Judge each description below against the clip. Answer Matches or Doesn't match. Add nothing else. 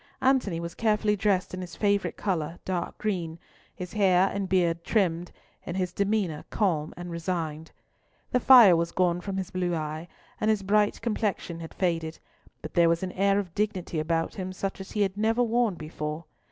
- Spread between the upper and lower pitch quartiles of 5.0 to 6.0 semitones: Doesn't match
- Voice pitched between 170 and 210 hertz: Matches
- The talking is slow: Doesn't match